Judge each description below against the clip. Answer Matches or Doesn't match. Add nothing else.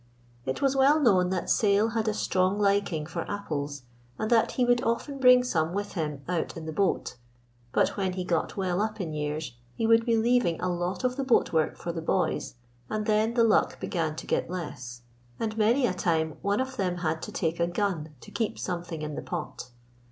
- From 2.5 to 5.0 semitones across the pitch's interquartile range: Doesn't match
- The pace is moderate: Doesn't match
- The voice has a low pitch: Doesn't match